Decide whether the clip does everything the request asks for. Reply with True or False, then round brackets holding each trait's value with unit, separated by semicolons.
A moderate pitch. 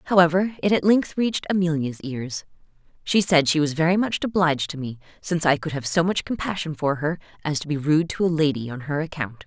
True (160 Hz)